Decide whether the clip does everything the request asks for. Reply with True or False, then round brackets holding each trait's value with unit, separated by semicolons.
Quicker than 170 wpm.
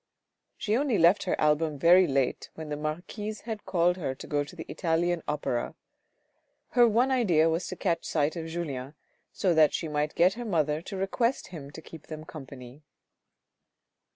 True (180 wpm)